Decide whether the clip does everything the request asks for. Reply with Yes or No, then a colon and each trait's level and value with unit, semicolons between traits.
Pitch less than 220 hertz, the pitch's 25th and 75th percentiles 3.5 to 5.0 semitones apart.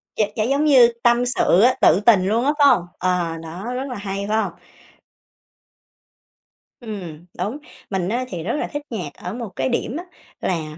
No: high, 210 Hz; wide, 5.5 semitones